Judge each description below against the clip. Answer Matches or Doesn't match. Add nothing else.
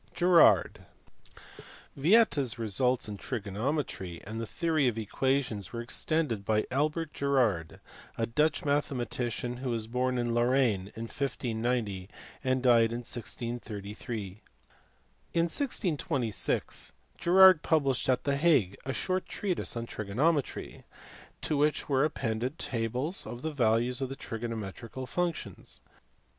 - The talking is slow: Matches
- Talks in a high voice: Doesn't match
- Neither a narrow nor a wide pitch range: Matches